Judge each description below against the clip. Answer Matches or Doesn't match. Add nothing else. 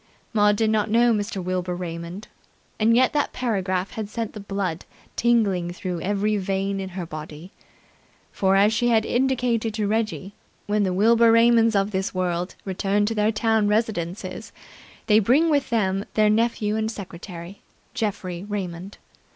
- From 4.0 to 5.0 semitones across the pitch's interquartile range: Doesn't match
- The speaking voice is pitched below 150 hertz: Doesn't match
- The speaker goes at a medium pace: Matches